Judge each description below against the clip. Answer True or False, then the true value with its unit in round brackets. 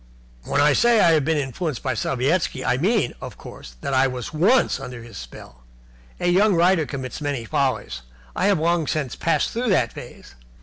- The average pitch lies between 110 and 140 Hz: False (150 Hz)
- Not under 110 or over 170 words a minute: False (190 wpm)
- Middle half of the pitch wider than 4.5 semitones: True (5.5 semitones)